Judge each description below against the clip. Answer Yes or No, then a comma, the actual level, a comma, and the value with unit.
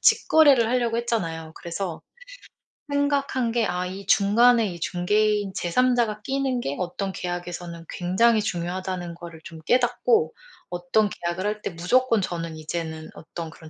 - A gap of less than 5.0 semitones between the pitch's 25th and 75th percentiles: No, wide, 5.4 semitones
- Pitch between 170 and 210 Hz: Yes, high, 190 Hz